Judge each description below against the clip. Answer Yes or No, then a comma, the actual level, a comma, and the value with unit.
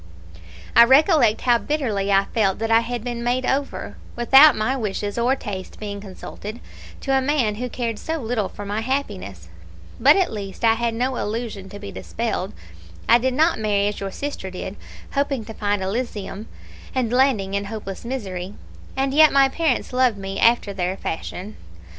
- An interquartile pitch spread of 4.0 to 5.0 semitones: Yes, average, 4.3 semitones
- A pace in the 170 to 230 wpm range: Yes, average, 175 wpm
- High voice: Yes, high, 225 Hz